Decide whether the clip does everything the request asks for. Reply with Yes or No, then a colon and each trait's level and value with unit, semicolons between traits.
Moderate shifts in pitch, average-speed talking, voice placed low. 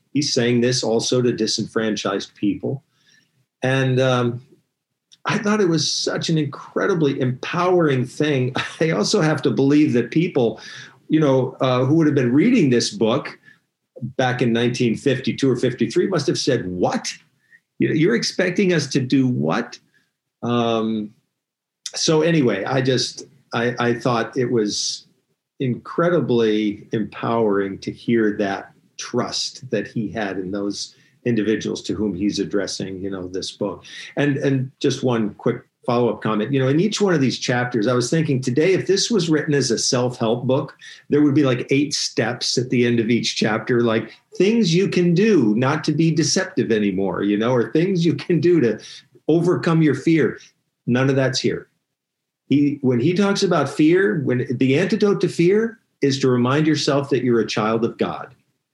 Yes: average, 4.9 semitones; average, 170 wpm; low, 130 Hz